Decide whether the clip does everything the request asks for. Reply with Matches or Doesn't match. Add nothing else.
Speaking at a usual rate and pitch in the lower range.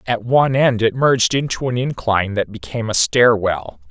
Matches